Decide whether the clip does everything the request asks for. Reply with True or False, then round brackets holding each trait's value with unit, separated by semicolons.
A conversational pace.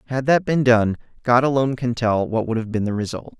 False (245 wpm)